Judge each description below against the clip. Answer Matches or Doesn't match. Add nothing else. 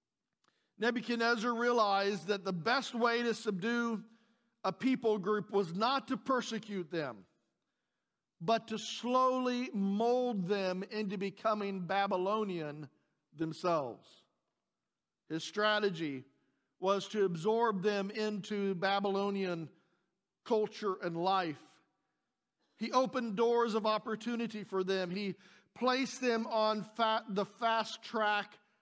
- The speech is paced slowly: Matches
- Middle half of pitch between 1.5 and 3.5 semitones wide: Matches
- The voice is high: Matches